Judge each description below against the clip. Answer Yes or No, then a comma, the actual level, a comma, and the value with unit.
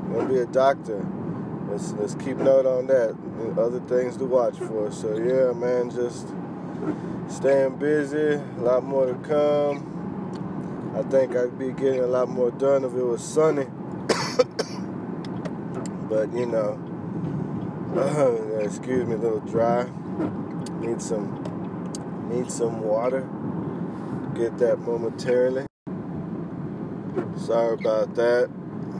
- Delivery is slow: Yes, slow, 120 wpm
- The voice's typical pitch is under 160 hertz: Yes, low, 135 Hz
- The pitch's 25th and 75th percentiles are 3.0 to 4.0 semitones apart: No, average, 4.5 semitones